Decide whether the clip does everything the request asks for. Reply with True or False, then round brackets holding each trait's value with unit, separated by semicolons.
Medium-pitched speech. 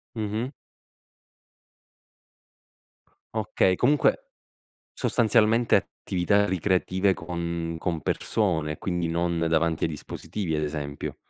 False (90 Hz)